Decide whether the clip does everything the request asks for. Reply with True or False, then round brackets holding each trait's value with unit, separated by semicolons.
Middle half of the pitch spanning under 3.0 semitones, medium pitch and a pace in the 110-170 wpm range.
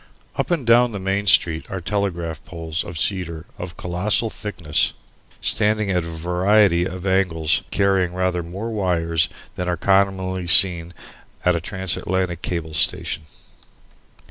False (2.5 semitones; 90 Hz; 145 wpm)